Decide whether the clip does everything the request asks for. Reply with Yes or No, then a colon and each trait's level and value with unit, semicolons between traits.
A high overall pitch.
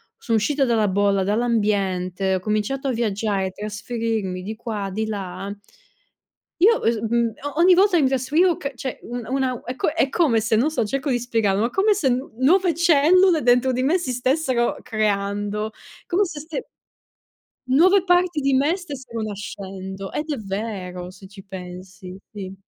Yes: high, 235 Hz